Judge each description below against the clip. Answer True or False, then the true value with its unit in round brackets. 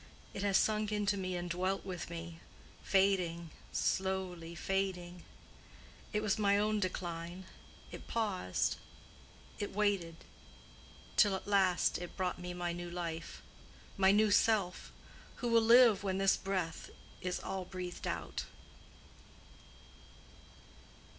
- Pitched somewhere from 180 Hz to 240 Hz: True (190 Hz)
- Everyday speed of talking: False (110 wpm)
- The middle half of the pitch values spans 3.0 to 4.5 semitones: False (2.4 semitones)